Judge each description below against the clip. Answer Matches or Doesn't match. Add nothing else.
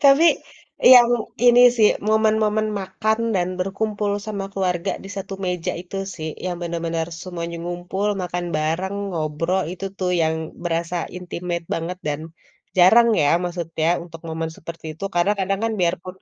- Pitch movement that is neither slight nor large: Matches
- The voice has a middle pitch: Matches